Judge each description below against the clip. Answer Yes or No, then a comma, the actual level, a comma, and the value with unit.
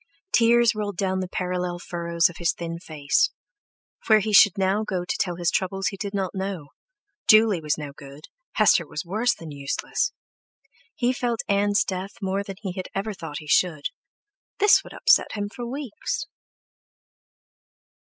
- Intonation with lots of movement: No, average, 3.7 semitones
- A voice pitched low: No, high, 190 Hz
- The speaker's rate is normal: Yes, average, 160 wpm